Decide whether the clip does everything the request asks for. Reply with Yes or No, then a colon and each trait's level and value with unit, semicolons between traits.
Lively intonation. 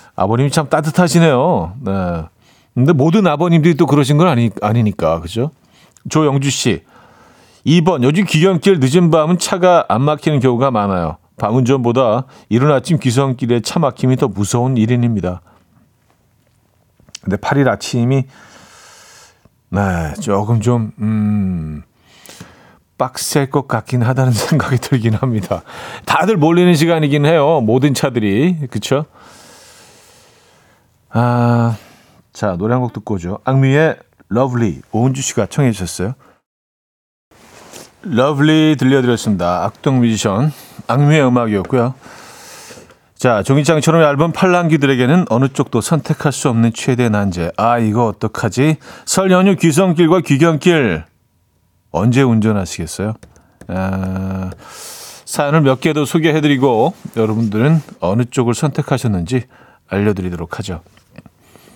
Yes: wide, 5.8 semitones